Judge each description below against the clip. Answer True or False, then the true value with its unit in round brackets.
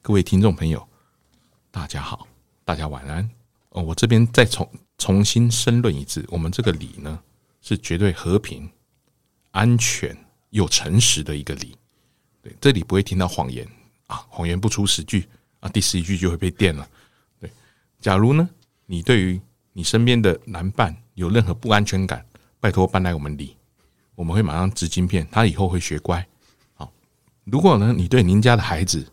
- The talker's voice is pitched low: True (95 Hz)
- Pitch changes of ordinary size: True (4.6 semitones)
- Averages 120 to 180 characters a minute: False (255 characters per minute)